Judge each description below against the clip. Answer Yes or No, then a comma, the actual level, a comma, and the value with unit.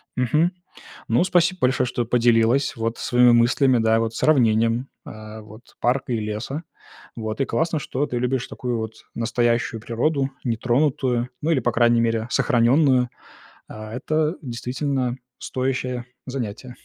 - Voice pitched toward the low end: Yes, low, 120 Hz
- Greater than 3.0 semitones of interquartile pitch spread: No, average, 2.7 semitones